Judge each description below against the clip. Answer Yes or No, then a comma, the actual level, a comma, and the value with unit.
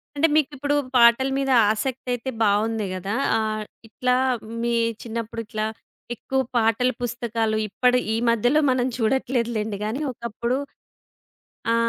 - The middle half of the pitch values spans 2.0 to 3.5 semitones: Yes, narrow, 2.5 semitones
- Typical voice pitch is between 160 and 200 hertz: No, high, 235 Hz